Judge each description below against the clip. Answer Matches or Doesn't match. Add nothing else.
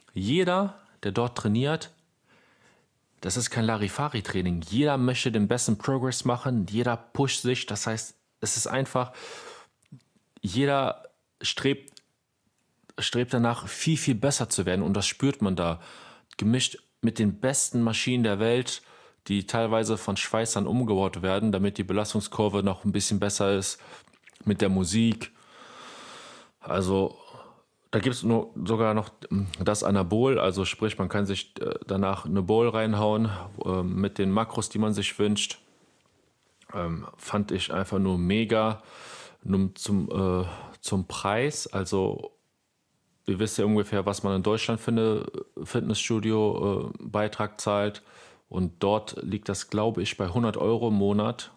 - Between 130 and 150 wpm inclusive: Matches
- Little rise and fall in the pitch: Doesn't match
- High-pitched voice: Doesn't match